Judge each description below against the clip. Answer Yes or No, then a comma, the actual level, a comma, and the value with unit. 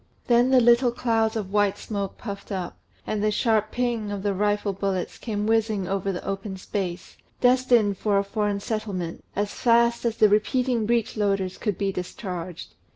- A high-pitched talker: Yes, high, 210 Hz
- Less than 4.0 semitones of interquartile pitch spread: Yes, average, 2.7 semitones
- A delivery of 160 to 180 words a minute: Yes, average, 175 wpm